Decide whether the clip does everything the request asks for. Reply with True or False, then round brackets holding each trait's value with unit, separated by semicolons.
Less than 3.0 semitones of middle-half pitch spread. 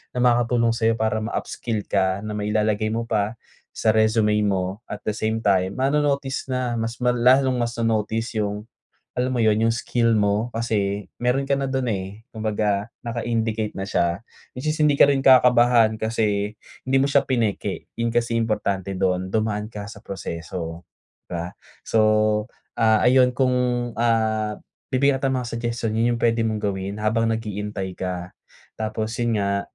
True (2.5 semitones)